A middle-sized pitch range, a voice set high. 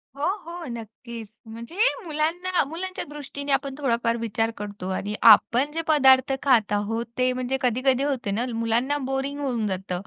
Yes: average, 4.0 semitones; very high, 255 Hz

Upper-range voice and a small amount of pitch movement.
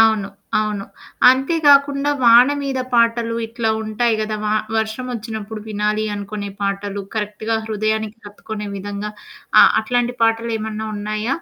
Yes: high, 220 Hz; narrow, 1.8 semitones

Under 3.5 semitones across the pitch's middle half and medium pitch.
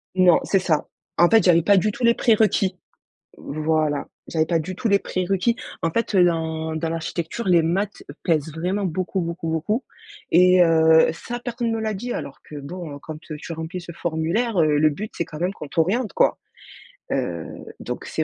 No: average, 3.8 semitones; medium, 175 Hz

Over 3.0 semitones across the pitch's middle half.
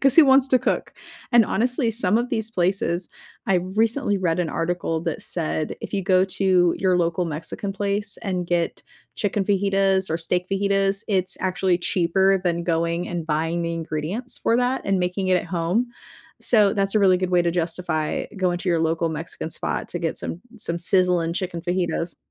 No: average, 2.7 semitones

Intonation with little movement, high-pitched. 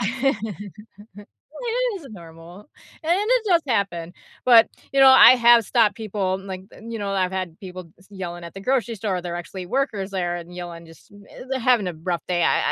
No: average, 4.9 semitones; high, 195 Hz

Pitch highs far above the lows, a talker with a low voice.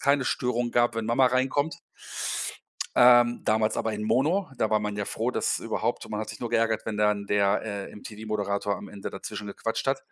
No: average, 2.8 semitones; low, 110 Hz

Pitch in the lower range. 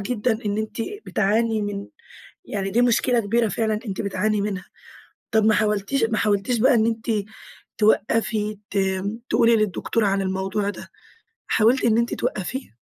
No: high, 215 Hz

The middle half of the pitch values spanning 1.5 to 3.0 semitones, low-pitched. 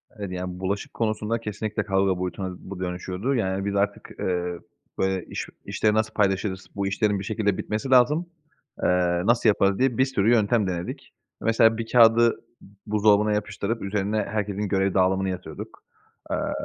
Yes: average, 2.7 semitones; low, 100 Hz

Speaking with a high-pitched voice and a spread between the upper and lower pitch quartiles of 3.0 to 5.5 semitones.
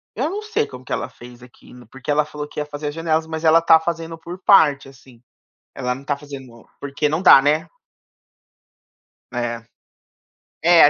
No: medium, 150 Hz; average, 3.8 semitones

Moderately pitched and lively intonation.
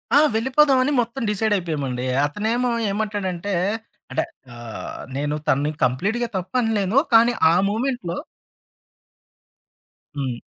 No: high, 205 Hz; wide, 8.1 semitones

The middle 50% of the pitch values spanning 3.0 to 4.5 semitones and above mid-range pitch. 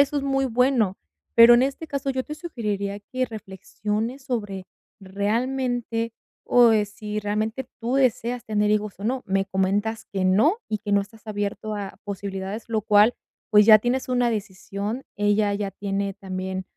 Yes: average, 3.4 semitones; high, 215 Hz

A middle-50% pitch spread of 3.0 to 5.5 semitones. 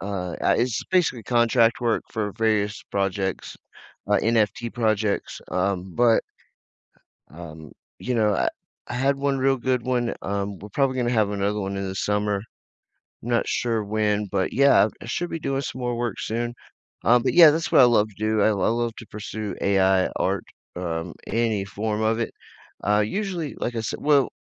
Yes: average, 3.3 semitones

